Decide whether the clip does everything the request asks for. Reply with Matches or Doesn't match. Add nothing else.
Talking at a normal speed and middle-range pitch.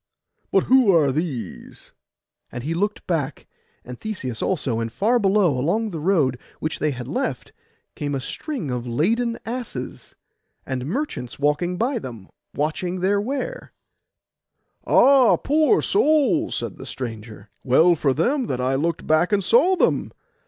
Matches